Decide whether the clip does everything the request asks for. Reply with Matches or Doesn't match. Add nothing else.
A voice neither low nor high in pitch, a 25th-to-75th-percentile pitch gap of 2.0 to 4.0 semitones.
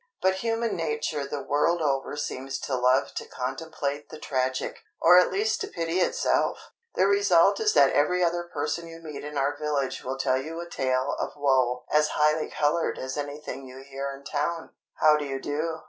Matches